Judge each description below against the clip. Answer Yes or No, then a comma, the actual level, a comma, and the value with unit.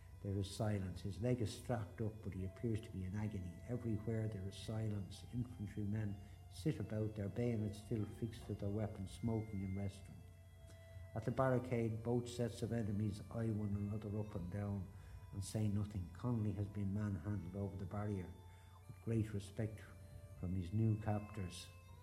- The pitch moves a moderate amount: No, narrow, 2.3 semitones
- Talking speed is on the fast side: No, average, 170 wpm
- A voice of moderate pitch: No, low, 105 Hz